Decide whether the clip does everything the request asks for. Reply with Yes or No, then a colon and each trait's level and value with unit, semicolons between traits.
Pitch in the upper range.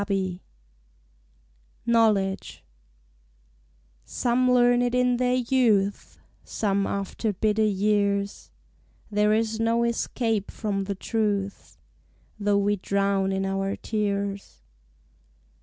Yes: high, 205 Hz